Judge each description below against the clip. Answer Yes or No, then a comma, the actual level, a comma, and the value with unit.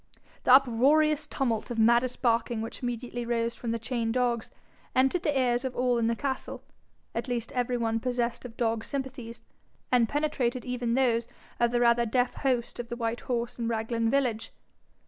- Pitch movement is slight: Yes, narrow, 1.7 semitones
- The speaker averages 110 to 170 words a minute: No, average, 180 wpm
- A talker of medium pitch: No, high, 240 Hz